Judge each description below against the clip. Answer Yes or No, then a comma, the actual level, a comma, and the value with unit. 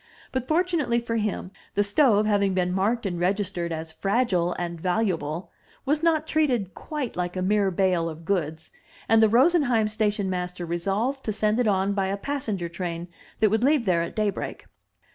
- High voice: Yes, high, 200 Hz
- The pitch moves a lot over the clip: No, average, 4.7 semitones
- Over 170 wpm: Yes, average, 180 wpm